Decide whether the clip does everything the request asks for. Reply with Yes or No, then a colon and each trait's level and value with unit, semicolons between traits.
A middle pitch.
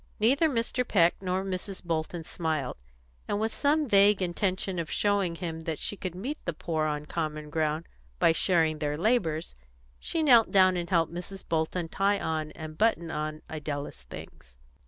Yes: medium, 170 Hz